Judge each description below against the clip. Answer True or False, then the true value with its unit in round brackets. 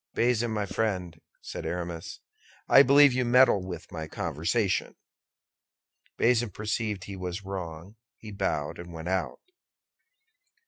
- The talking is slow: True (125 wpm)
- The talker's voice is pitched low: True (100 Hz)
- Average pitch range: True (4.7 semitones)